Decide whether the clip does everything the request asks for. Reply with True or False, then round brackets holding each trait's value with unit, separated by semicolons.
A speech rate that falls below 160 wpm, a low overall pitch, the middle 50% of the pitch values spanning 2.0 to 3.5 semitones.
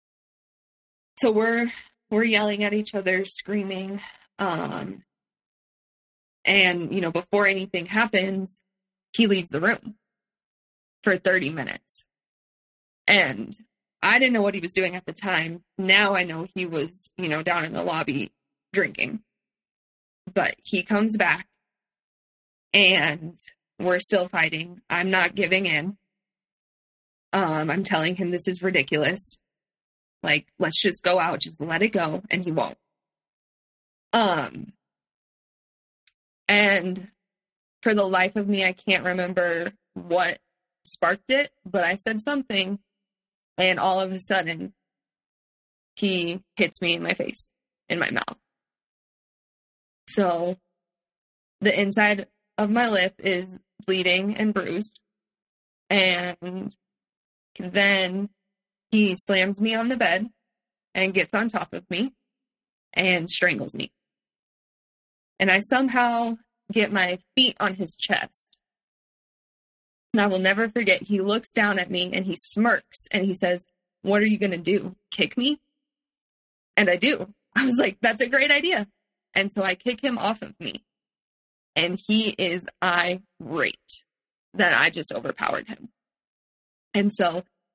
False (135 wpm; 195 Hz; 2.9 semitones)